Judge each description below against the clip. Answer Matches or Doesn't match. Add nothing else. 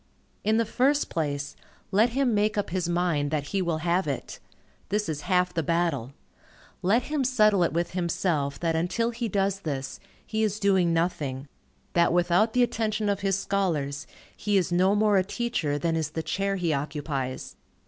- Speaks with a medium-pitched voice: Matches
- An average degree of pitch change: Matches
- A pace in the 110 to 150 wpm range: Doesn't match